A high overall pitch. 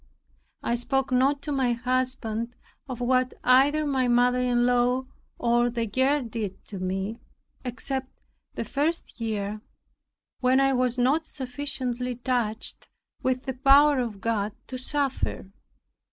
Yes: very high, 250 Hz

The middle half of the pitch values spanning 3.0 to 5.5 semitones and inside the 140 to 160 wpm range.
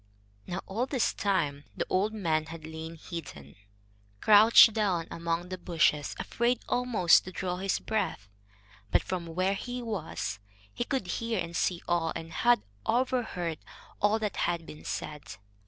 Yes: average, 4.9 semitones; average, 155 wpm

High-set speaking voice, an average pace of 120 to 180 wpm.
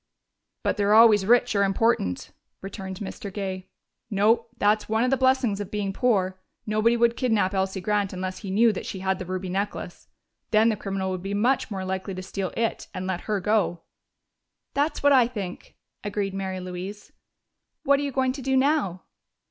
No: high, 205 Hz; average, 190 wpm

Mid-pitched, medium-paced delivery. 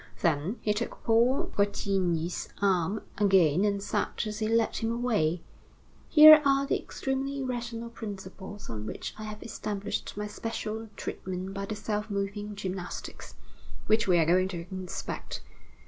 No: high, 205 Hz; average, 145 wpm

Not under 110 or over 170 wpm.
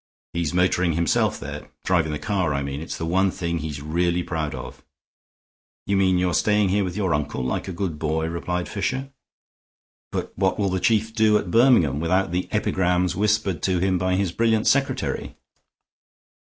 No: average, 180 wpm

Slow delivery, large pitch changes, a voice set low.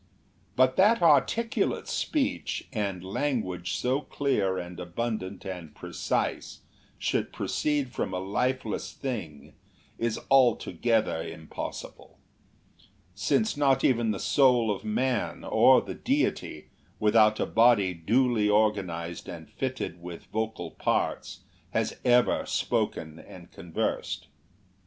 Yes: slow, 110 wpm; wide, 5.7 semitones; low, 110 Hz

